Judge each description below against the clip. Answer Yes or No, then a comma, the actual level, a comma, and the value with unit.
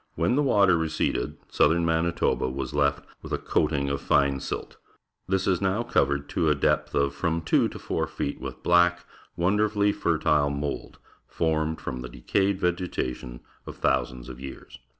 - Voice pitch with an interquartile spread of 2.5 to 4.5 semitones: Yes, average, 4.1 semitones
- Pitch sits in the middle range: No, very low, 80 Hz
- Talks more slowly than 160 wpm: No, average, 165 wpm